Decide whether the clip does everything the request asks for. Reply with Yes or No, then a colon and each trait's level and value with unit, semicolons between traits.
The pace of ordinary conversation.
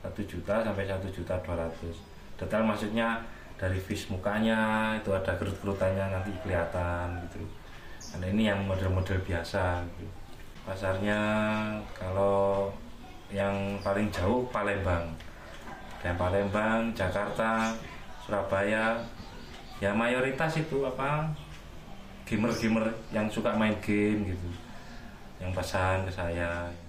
Yes: average, 110 wpm